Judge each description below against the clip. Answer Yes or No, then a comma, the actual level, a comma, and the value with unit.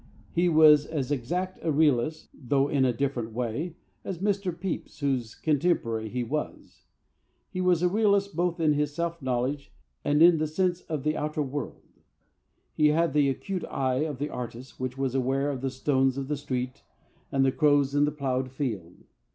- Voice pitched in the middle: Yes, medium, 145 Hz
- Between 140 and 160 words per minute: No, average, 185 wpm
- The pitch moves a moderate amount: Yes, average, 3.6 semitones